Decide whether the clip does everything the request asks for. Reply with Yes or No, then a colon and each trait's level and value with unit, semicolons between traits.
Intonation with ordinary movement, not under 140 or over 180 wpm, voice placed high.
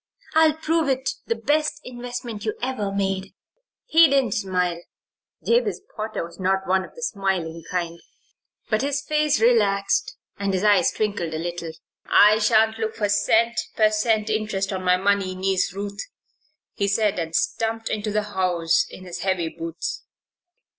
Yes: average, 3.5 semitones; average, 160 wpm; high, 205 Hz